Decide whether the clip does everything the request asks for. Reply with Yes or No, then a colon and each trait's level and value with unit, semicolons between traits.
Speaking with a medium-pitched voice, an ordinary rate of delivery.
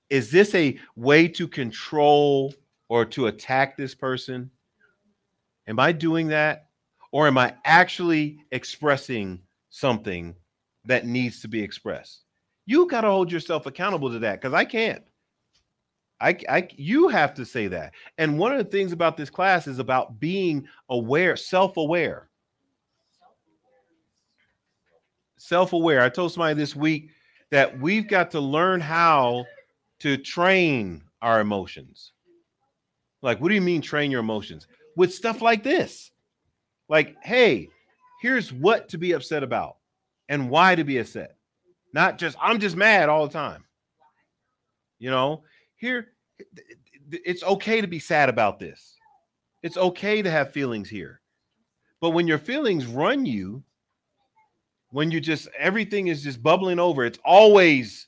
Yes: medium, 155 Hz; average, 145 wpm